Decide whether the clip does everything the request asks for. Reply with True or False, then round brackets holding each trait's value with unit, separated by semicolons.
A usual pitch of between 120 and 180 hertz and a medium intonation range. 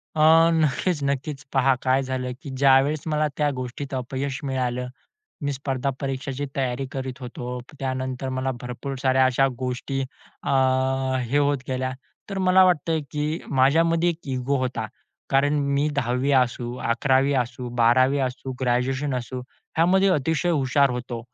False (135 Hz; 2.0 semitones)